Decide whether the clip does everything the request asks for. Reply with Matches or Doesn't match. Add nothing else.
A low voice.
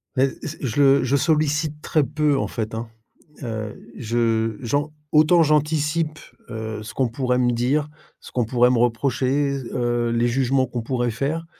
Matches